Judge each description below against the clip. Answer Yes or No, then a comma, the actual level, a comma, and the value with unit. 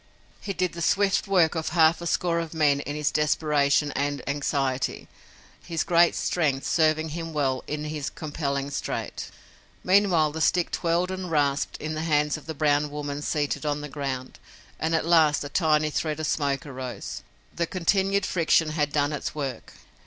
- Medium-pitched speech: Yes, medium, 155 Hz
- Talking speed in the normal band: Yes, average, 175 wpm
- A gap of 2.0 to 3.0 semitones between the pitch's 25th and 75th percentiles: Yes, narrow, 2.5 semitones